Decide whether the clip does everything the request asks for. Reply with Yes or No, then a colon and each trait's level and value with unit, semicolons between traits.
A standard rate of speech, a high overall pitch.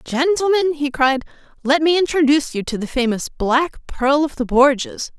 Yes: average, 175 wpm; very high, 285 Hz